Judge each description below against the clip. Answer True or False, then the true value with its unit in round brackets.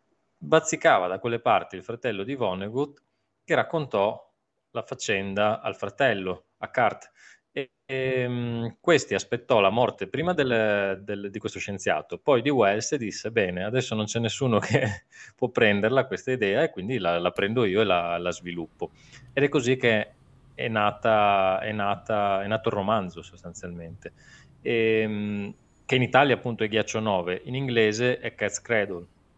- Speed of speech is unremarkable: True (160 wpm)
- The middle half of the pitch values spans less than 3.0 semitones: False (4.6 semitones)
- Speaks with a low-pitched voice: True (110 Hz)